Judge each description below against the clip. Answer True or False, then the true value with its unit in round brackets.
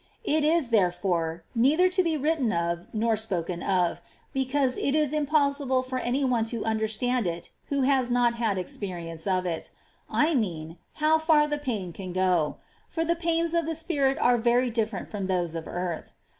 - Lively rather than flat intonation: True (8.0 semitones)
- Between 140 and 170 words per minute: False (185 wpm)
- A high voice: True (240 Hz)